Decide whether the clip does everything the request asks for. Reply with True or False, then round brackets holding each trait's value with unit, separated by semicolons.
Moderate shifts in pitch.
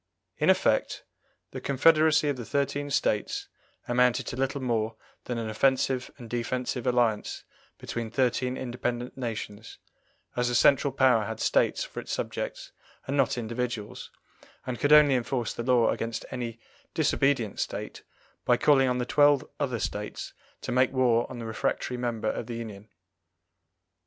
False (2.3 semitones)